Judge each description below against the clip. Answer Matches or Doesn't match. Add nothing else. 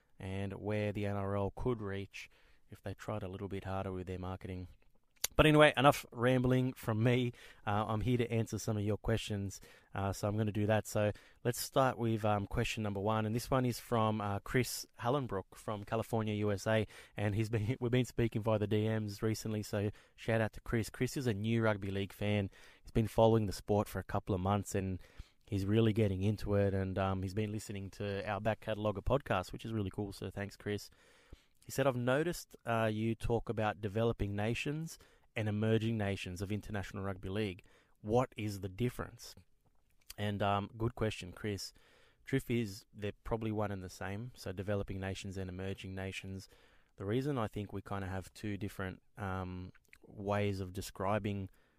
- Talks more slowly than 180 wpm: Doesn't match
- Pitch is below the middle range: Matches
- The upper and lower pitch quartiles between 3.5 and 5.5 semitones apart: Doesn't match